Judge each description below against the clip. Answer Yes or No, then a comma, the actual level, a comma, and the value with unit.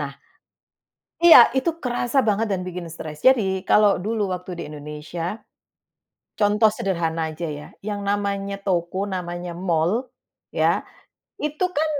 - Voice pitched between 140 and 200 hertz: Yes, high, 190 Hz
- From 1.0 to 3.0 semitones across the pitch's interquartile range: No, average, 3.9 semitones